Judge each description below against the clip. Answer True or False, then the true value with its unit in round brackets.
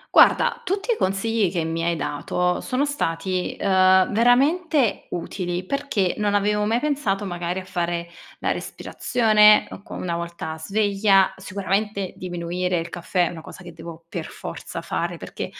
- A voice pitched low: False (190 Hz)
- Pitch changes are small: False (3.6 semitones)